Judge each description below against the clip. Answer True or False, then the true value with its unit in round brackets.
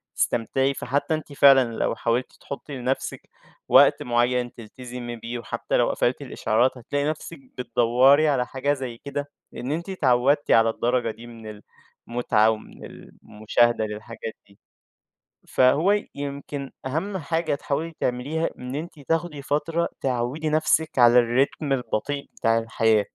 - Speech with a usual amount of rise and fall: True (3.4 semitones)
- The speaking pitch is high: False (130 Hz)